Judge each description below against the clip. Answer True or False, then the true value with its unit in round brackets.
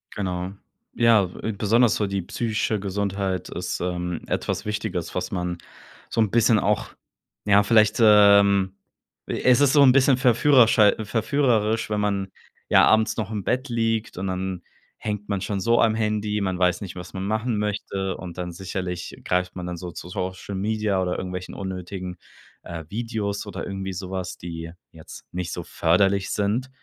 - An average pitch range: True (3.0 semitones)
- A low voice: True (100 Hz)